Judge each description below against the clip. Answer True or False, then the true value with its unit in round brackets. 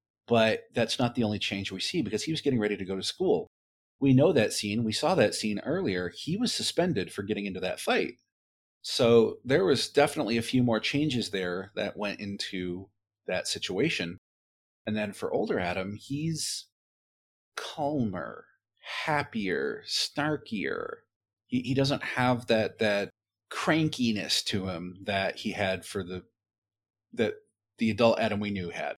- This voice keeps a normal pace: True (160 wpm)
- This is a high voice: False (105 Hz)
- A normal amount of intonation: True (4.2 semitones)